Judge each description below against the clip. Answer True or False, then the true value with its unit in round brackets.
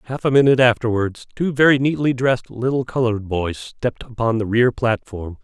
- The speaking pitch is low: True (120 Hz)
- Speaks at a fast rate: False (175 wpm)